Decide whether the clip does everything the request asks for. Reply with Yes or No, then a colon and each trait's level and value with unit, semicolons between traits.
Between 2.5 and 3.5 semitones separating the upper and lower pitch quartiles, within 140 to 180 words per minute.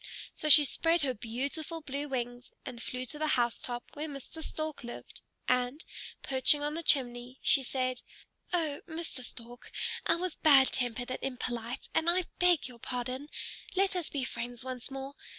No: average, 3.9 semitones; average, 170 wpm